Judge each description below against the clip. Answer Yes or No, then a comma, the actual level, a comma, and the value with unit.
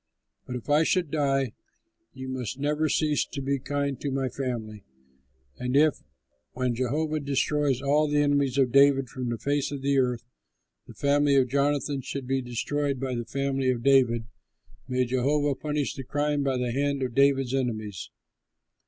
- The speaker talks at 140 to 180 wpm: Yes, average, 170 wpm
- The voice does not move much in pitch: Yes, narrow, 2.1 semitones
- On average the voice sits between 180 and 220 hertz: No, low, 135 Hz